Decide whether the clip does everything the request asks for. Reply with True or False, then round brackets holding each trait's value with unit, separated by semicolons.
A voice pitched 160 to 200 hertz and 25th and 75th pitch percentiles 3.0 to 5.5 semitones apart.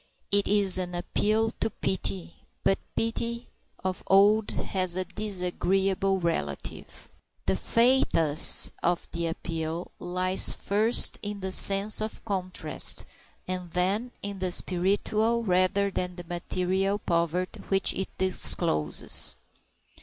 False (185 Hz; 2.4 semitones)